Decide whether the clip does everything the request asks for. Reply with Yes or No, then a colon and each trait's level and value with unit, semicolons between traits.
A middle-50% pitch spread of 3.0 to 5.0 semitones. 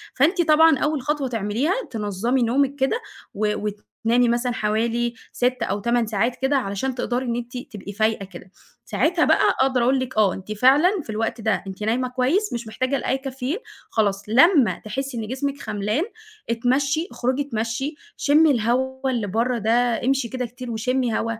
Yes: average, 3.4 semitones